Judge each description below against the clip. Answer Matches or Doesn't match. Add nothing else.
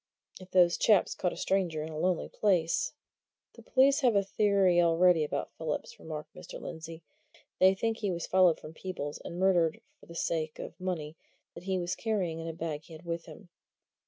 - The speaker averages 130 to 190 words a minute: Doesn't match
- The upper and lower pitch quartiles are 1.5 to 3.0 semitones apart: Matches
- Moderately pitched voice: Matches